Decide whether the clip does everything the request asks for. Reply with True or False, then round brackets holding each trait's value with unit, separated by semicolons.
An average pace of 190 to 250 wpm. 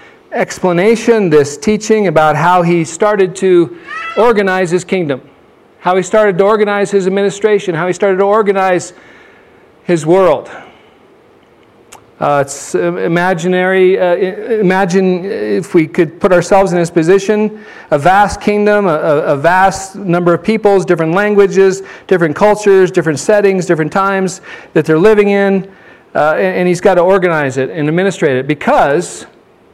False (140 wpm)